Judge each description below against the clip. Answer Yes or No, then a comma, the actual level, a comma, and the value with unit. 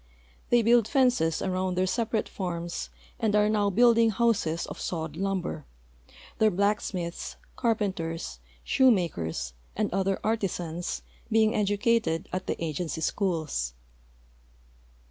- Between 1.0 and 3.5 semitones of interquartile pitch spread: No, average, 4.6 semitones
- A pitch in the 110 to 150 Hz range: No, high, 195 Hz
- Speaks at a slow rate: Yes, slow, 110 wpm